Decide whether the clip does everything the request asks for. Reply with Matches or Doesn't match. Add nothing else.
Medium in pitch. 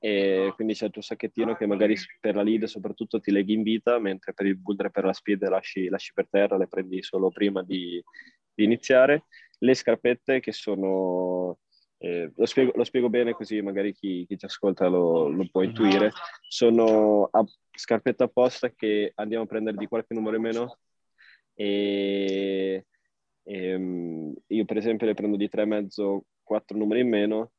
Doesn't match